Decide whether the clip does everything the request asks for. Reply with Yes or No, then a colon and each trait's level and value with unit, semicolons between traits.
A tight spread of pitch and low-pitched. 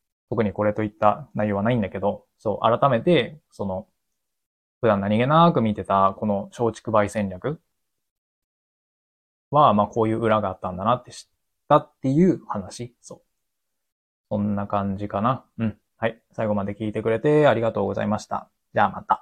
Yes: narrow, 2.3 semitones; low, 105 Hz